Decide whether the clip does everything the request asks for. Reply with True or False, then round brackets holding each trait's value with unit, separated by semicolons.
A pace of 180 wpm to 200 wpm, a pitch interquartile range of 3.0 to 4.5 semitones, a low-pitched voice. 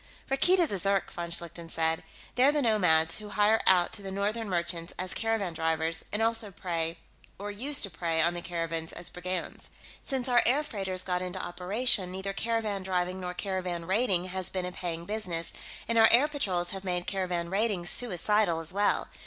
False (190 wpm; 3.5 semitones; 185 Hz)